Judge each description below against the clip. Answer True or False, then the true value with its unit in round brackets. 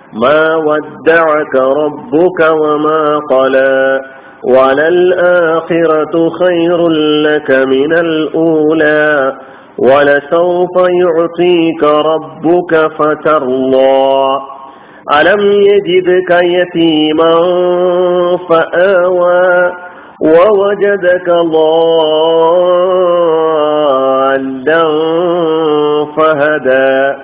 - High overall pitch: False (160 Hz)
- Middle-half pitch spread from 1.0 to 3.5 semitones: True (2.8 semitones)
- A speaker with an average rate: False (45 wpm)